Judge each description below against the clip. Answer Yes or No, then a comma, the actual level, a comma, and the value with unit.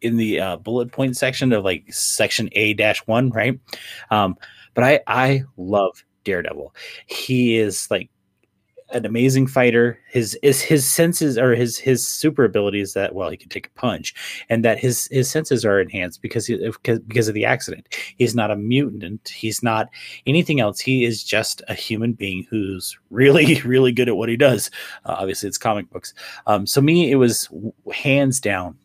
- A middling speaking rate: Yes, average, 180 wpm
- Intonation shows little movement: No, average, 3.4 semitones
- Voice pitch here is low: Yes, low, 120 Hz